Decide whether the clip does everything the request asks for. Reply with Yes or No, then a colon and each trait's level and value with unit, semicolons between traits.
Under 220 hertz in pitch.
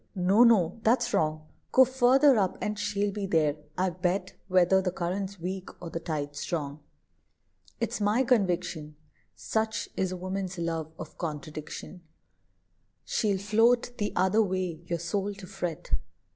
Yes: medium, 185 Hz